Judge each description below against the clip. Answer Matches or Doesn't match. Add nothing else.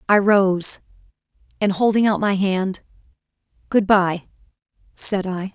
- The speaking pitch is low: Doesn't match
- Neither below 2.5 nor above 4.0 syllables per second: Matches